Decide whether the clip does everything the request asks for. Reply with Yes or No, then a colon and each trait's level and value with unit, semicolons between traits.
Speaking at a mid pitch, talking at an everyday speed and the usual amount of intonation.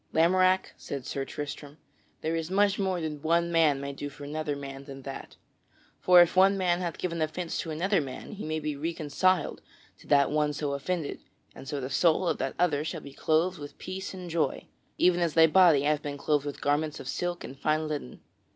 No: medium, 155 Hz; fast, 210 wpm; average, 3.4 semitones